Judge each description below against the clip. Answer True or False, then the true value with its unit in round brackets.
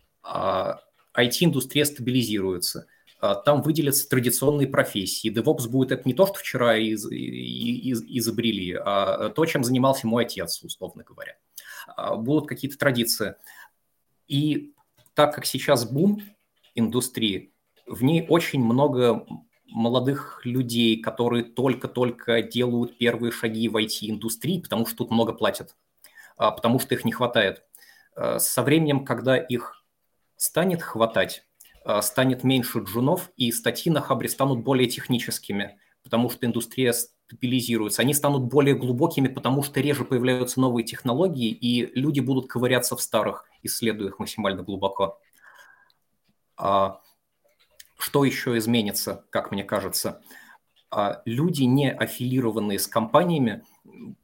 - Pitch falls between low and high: False (125 Hz)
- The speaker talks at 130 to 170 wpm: False (120 wpm)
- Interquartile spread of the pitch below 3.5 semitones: True (3.0 semitones)